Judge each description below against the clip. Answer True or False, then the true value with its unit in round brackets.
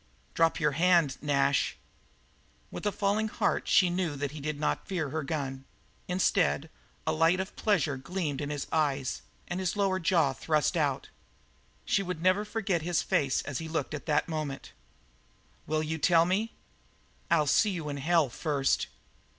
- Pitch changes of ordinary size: True (4.0 semitones)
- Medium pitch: True (160 Hz)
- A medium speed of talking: True (170 wpm)